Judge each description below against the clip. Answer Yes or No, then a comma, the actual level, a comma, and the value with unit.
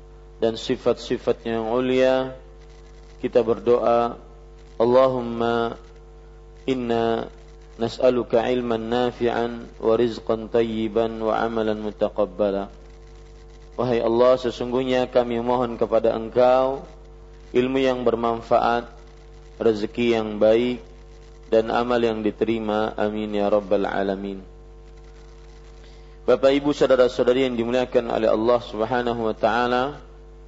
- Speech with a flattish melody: Yes, narrow, 1.8 semitones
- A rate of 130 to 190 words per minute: No, average, 95 wpm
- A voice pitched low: Yes, low, 115 Hz